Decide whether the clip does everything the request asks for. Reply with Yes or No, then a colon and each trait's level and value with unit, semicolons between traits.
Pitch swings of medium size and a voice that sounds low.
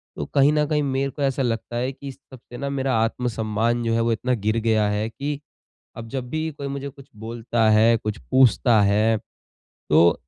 Yes: average, 3.5 semitones; low, 120 Hz